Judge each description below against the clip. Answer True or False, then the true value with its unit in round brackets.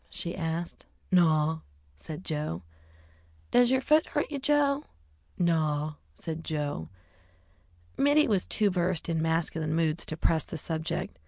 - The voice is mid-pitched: True (165 Hz)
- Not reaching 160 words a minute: True (135 wpm)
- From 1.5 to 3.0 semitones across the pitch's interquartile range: False (4.1 semitones)